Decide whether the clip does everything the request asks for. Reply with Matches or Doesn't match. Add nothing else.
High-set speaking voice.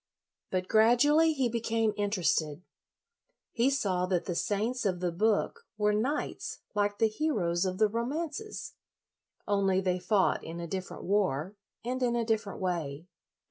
Matches